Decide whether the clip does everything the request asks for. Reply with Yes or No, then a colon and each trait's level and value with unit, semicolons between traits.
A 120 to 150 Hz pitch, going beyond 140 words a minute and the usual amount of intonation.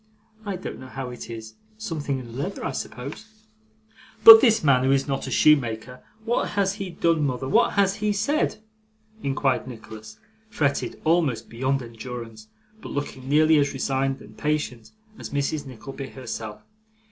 Yes: low, 135 Hz; average, 160 wpm; average, 4.1 semitones